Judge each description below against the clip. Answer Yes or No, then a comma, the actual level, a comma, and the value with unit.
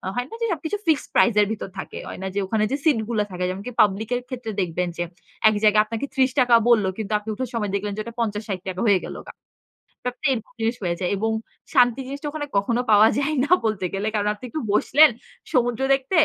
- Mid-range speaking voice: No, high, 225 Hz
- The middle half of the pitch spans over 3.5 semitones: Yes, average, 3.9 semitones